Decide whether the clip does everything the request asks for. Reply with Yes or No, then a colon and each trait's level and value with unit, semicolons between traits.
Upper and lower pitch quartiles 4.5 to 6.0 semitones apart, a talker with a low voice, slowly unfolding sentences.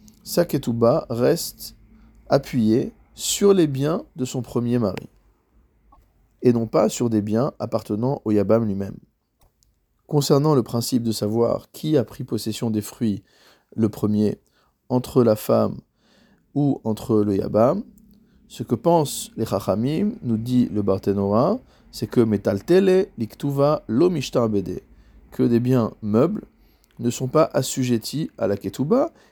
Yes: average, 5.0 semitones; low, 120 Hz; slow, 130 wpm